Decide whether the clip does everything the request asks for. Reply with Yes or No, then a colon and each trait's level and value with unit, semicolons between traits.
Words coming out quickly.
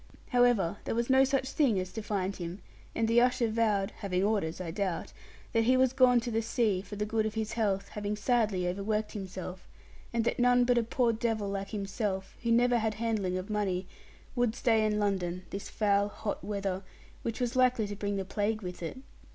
Yes: fast, 210 wpm